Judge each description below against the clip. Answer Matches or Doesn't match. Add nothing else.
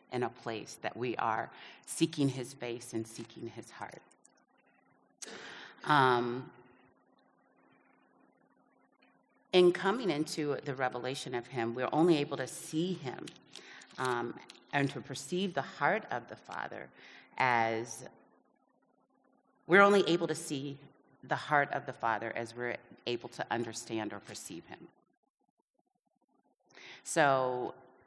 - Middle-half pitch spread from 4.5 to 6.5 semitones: Matches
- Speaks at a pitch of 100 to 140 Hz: Matches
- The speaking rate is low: Matches